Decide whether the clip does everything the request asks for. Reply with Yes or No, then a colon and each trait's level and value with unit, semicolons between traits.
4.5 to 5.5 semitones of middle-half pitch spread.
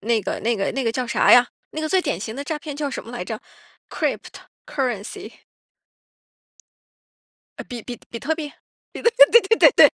Yes: average, 5.1 semitones